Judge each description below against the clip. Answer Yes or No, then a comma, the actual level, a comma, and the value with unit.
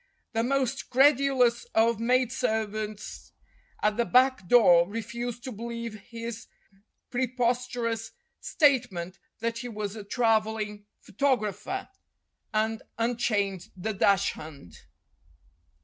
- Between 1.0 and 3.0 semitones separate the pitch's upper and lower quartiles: Yes, average, 2.7 semitones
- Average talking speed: No, slow, 105 wpm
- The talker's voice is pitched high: Yes, high, 230 Hz